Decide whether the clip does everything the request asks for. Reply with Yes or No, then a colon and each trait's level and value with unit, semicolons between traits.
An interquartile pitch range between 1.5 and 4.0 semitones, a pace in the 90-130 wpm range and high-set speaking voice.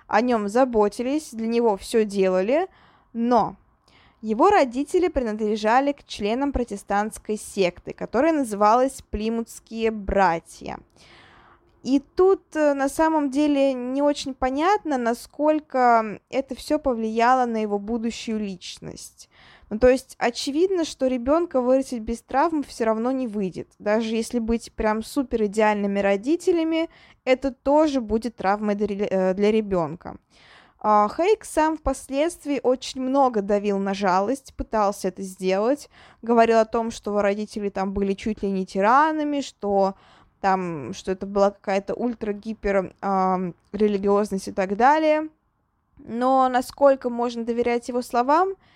No: average, 4.9 semitones; average, 125 wpm; high, 230 Hz